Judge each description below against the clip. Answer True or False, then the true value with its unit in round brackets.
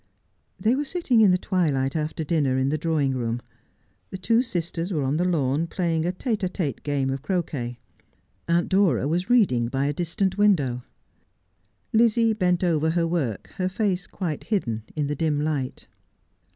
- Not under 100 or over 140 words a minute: False (180 wpm)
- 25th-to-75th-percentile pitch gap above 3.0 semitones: True (5.0 semitones)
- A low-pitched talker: False (165 Hz)